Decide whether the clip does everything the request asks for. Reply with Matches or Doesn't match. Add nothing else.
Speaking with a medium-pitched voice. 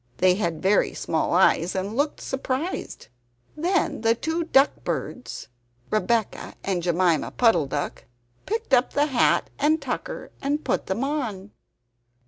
Doesn't match